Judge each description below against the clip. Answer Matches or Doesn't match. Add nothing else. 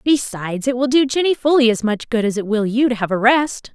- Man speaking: Doesn't match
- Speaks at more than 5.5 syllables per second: Matches